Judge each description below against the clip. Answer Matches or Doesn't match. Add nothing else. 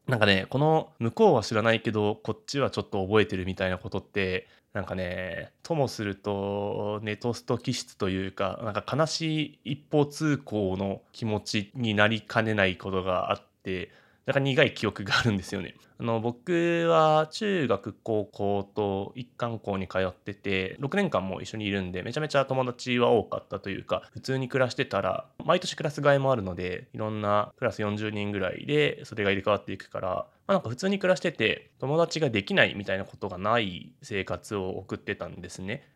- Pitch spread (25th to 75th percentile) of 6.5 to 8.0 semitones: Doesn't match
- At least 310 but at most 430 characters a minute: Matches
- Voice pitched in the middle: Doesn't match